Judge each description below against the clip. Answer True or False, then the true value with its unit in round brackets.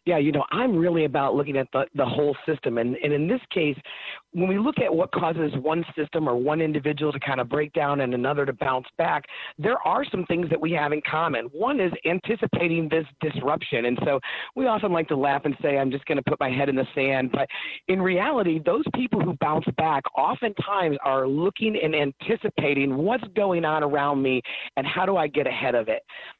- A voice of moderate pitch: True (155 Hz)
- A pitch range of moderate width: True (4.2 semitones)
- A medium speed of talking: False (220 wpm)